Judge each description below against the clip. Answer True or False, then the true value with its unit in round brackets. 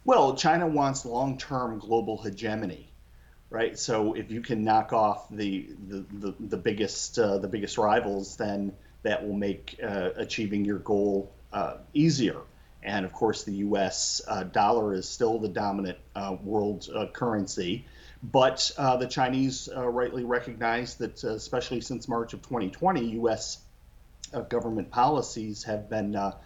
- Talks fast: False (155 wpm)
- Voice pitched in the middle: False (110 Hz)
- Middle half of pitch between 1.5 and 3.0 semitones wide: False (3.5 semitones)